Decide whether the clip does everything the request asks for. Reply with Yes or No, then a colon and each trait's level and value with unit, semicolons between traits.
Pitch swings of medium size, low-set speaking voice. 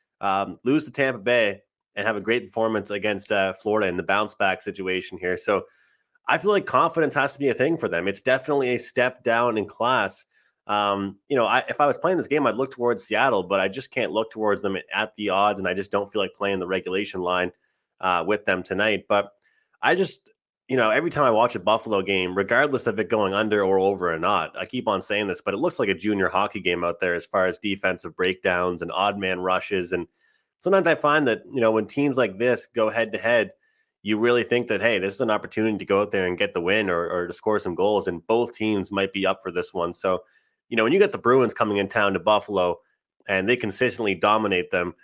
Yes: average, 4.2 semitones; low, 105 Hz